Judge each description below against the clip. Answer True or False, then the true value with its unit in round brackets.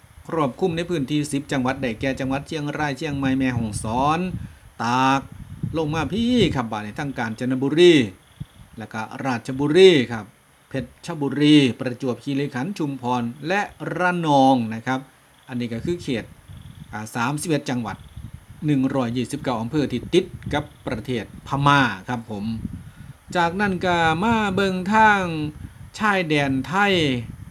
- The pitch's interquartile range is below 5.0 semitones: True (4.5 semitones)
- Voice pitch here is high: False (135 Hz)